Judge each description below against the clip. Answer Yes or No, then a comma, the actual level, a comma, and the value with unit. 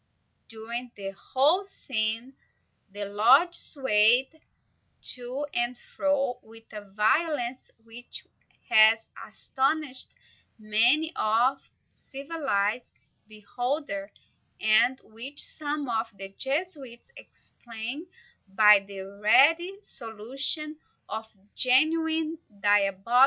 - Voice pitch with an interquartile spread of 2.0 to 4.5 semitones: No, average, 5.0 semitones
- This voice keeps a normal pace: No, slow, 95 wpm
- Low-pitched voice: No, high, 245 Hz